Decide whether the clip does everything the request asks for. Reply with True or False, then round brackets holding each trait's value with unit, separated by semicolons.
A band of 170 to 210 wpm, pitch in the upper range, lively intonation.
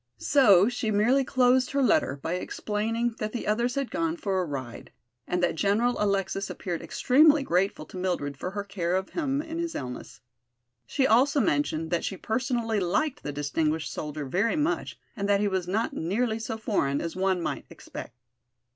True (180 wpm; 205 Hz; 6.0 semitones)